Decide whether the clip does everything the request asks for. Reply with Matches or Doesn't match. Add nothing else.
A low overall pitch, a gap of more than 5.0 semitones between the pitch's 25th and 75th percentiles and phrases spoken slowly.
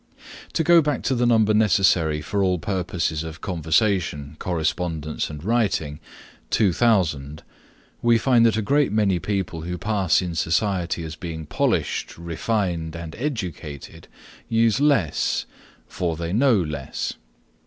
Matches